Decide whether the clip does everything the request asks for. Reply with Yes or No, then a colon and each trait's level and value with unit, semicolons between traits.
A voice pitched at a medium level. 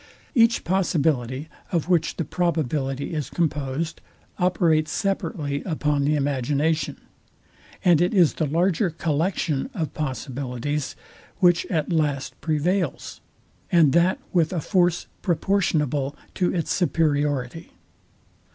Yes: medium, 160 Hz